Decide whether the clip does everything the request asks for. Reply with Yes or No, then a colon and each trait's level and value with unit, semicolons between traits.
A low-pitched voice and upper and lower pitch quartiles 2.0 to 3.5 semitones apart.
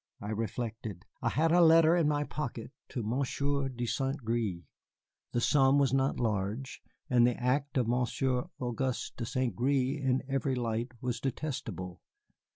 Yes: low, 125 Hz; average, 3.0 semitones